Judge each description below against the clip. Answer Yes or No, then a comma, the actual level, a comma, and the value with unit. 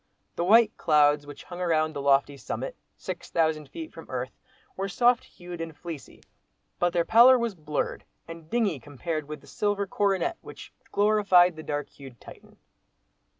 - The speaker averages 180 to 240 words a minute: No, average, 160 wpm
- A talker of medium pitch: Yes, medium, 170 Hz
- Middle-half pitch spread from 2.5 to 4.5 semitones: No, average, 5.3 semitones